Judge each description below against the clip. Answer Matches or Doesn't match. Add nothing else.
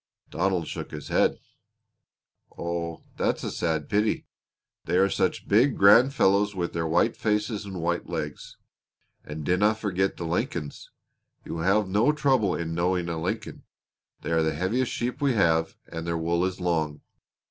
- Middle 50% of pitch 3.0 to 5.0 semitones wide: Matches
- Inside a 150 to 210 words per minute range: Matches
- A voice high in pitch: Doesn't match